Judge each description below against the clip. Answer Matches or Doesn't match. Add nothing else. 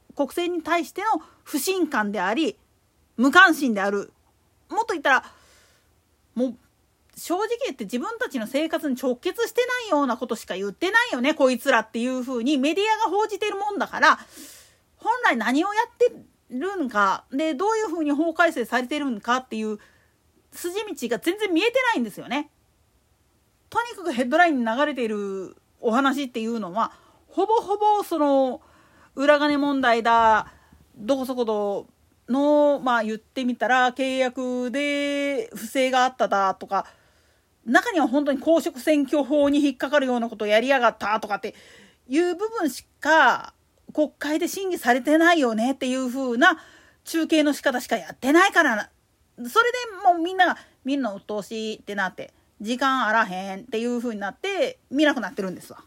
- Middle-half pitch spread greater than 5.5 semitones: Matches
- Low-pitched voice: Doesn't match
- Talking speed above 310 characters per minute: Matches